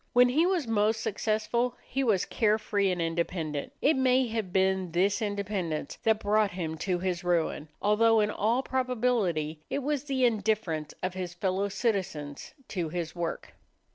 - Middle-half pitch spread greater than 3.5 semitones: Yes, average, 4.6 semitones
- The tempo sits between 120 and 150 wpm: No, average, 160 wpm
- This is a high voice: Yes, high, 205 Hz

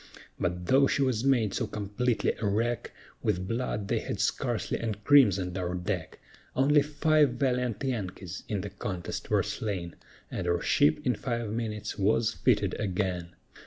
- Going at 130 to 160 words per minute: Yes, average, 155 wpm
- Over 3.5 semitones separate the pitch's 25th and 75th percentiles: Yes, average, 5.0 semitones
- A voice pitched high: No, low, 105 Hz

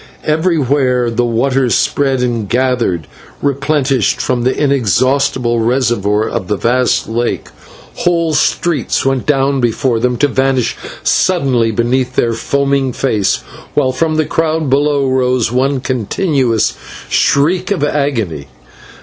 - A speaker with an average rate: No, slow, 125 wpm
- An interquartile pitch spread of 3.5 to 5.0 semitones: No, average, 3.0 semitones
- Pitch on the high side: No, low, 130 Hz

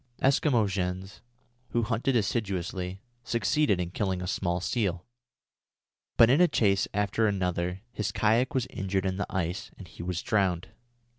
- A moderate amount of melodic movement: Yes, average, 3.8 semitones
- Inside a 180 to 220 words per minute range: No, average, 150 wpm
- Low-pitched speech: Yes, low, 100 Hz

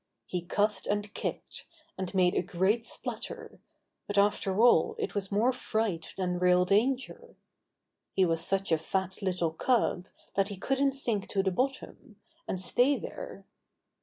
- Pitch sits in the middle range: No, high, 200 Hz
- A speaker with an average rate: Yes, average, 155 wpm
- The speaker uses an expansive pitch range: No, average, 4.9 semitones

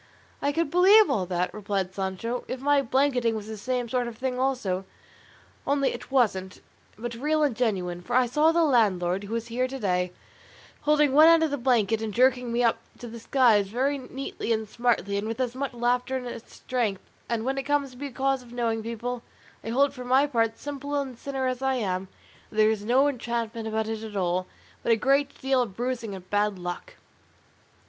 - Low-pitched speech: No, high, 240 Hz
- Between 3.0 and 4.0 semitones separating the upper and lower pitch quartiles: Yes, average, 3.7 semitones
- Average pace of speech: No, fast, 210 wpm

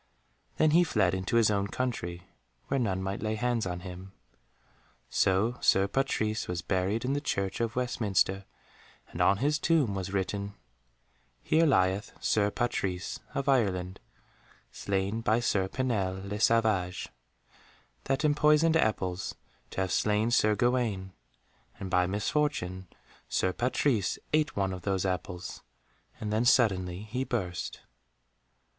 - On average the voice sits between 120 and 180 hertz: No, low, 105 Hz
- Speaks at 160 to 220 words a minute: No, slow, 135 wpm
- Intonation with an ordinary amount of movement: Yes, average, 4.6 semitones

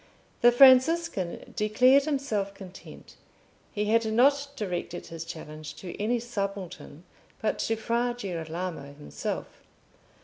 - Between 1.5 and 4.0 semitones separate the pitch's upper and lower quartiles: No, wide, 5.6 semitones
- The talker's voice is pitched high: Yes, high, 210 Hz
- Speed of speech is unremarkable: No, slow, 110 wpm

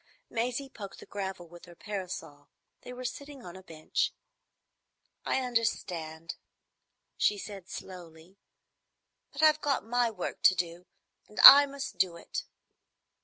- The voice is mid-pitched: No, high, 195 Hz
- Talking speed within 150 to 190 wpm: No, slow, 135 wpm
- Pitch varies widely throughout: Yes, wide, 6.3 semitones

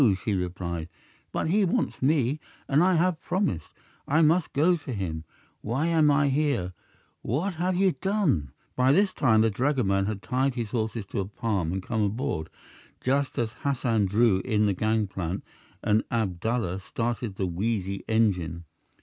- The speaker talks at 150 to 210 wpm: Yes, average, 160 wpm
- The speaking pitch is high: No, low, 115 Hz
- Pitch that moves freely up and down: Yes, wide, 6.8 semitones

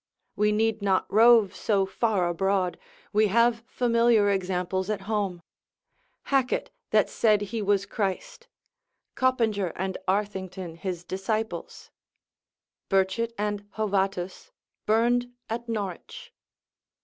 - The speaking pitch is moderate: No, high, 205 Hz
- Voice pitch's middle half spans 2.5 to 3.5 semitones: Yes, average, 2.9 semitones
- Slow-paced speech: Yes, slow, 105 wpm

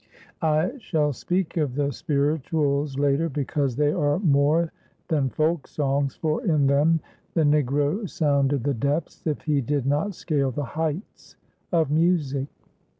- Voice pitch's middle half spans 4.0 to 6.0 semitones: No, narrow, 2.4 semitones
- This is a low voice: No, medium, 150 Hz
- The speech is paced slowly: No, average, 145 wpm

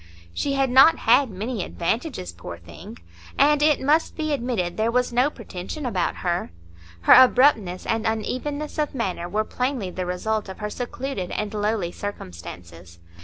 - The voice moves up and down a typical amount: No, wide, 6.7 semitones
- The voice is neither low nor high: No, high, 220 Hz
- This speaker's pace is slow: No, average, 160 wpm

